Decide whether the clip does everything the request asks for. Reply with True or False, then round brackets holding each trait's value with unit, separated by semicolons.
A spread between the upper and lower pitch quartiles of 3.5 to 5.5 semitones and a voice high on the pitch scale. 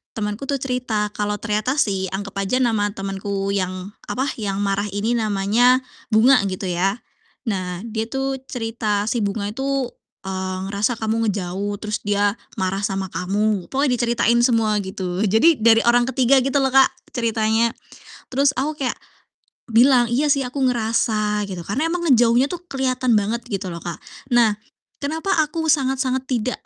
True (4.2 semitones; 225 Hz)